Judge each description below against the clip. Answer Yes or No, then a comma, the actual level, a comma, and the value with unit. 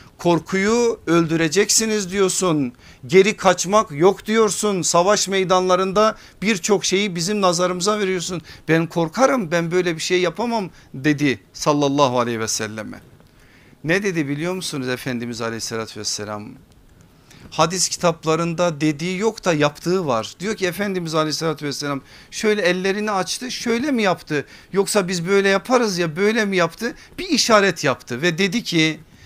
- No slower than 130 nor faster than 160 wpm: Yes, average, 135 wpm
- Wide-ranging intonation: No, average, 4.8 semitones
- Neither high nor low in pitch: Yes, medium, 180 Hz